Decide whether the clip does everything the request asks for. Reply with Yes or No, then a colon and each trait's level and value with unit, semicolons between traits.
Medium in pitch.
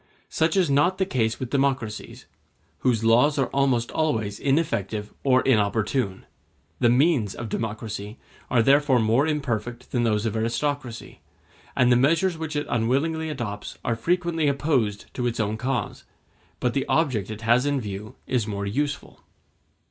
No: low, 125 Hz